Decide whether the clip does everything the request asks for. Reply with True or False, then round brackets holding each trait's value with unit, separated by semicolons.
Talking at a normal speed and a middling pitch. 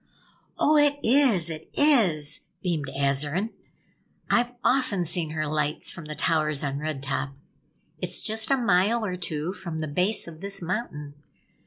True (155 wpm; 170 Hz)